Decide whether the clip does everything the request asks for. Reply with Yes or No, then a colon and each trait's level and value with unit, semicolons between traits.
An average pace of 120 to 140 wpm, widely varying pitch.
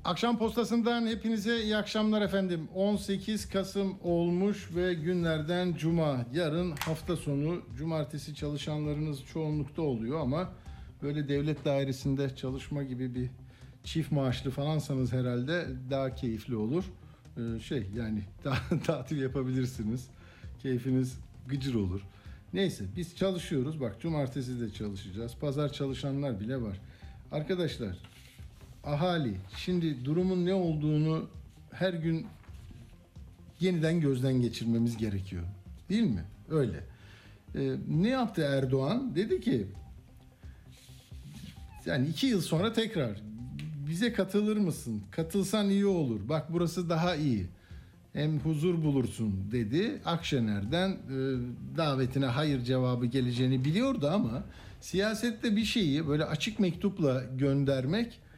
No: average, 110 wpm; wide, 6.2 semitones